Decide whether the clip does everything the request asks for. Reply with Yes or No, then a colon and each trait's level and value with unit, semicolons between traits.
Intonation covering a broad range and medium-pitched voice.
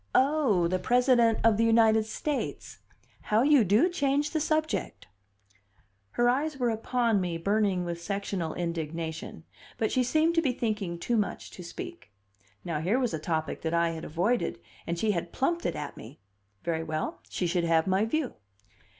No: wide, 6.9 semitones; high, 215 Hz